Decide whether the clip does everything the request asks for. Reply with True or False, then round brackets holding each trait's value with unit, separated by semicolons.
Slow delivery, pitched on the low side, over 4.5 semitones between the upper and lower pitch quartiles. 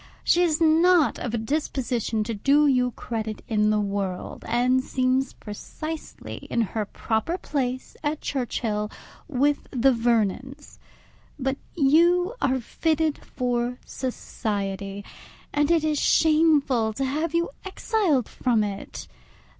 False (125 wpm; 260 Hz; 5.4 semitones)